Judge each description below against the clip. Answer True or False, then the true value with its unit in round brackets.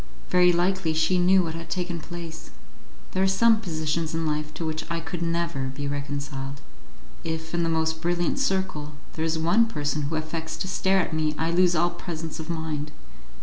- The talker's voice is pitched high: False (165 Hz)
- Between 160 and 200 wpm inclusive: True (190 wpm)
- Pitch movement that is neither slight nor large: False (2.1 semitones)